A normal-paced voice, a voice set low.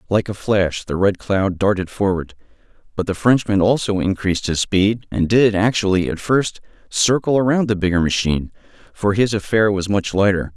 Yes: average, 175 wpm; low, 100 Hz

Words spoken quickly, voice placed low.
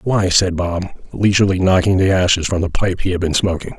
Yes: fast, 220 wpm; very low, 90 Hz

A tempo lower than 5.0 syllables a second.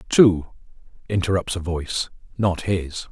Yes: 4.3 syllables/s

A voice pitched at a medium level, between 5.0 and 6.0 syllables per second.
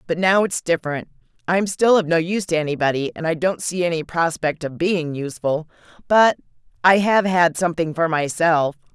Yes: medium, 170 Hz; 5.4 syllables/s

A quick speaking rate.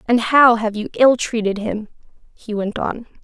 No: average, 185 wpm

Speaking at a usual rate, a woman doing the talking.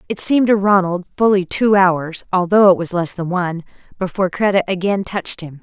Yes: average, 190 wpm; female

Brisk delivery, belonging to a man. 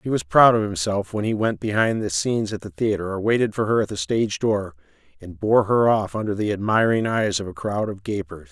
Yes: fast, 245 wpm; male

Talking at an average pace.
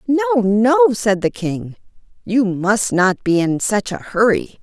Yes: average, 170 wpm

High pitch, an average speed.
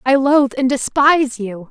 Yes: very high, 265 Hz; average, 175 wpm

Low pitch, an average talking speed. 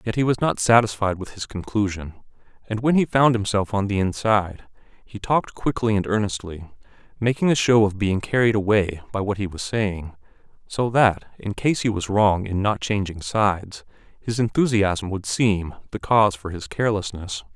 Yes: low, 105 Hz; average, 180 wpm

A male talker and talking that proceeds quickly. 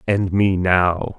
No: male; average, 150 wpm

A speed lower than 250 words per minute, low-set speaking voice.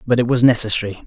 Yes: fast, 225 wpm; low, 115 Hz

